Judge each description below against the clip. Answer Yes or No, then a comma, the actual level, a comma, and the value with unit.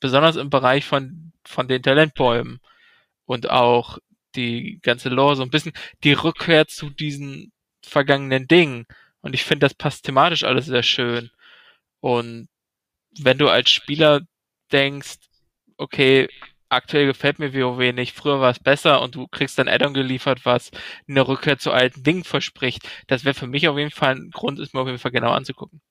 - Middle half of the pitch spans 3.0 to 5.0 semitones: No, narrow, 2.5 semitones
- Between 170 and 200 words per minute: Yes, average, 175 wpm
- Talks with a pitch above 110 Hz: Yes, low, 135 Hz